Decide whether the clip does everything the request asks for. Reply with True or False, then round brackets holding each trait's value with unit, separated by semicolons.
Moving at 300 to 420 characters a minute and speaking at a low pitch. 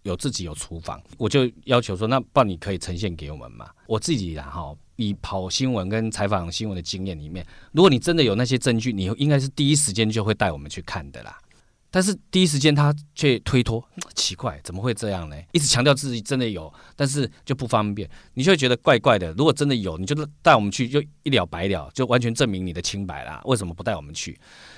True (345 characters per minute; 110 Hz)